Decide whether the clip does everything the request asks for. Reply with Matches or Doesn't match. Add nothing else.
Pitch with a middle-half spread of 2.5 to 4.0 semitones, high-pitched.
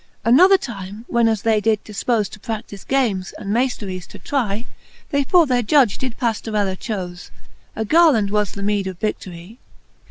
Matches